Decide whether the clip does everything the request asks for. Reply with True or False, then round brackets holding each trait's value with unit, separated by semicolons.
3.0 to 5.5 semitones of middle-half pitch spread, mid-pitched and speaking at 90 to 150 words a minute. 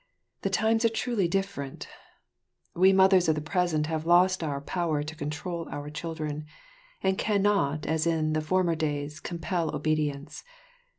True (3.6 semitones; 160 Hz; 140 wpm)